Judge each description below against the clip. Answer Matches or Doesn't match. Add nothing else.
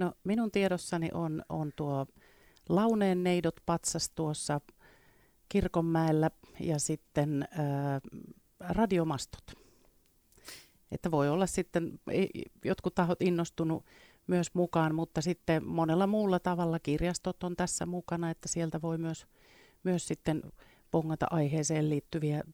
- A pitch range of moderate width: Doesn't match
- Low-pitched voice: Doesn't match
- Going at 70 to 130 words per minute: Matches